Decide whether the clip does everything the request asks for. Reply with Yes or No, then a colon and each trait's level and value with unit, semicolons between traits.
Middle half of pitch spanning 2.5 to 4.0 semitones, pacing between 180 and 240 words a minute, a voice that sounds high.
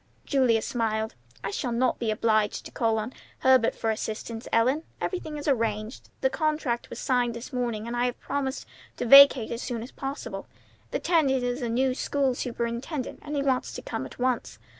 Yes: average, 2.9 semitones; average, 190 wpm; high, 245 Hz